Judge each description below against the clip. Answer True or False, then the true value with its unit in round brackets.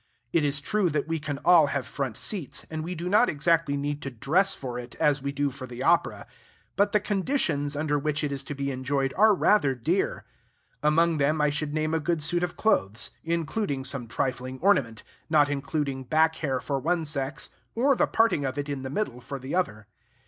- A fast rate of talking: True (210 wpm)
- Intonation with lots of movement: False (3.5 semitones)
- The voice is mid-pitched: True (145 Hz)